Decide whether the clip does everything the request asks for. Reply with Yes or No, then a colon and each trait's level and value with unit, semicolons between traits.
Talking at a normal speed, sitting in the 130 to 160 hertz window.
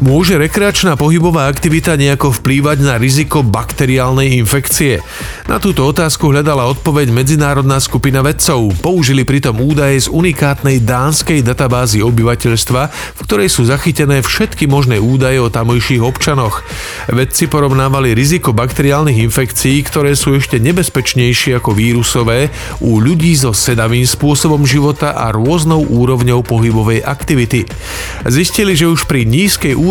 Yes: average, 125 wpm; low, 135 Hz